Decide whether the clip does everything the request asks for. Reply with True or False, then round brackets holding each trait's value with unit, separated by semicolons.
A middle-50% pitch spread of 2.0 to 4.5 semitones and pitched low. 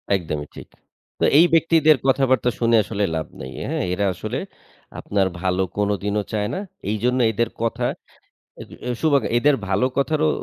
False (5.4 semitones; 115 Hz)